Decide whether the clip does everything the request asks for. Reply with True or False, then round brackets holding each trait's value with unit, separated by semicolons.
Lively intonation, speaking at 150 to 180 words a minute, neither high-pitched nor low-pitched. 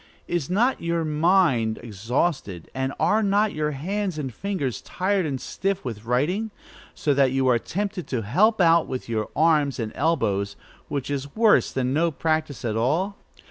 True (6.4 semitones; 170 wpm; 150 Hz)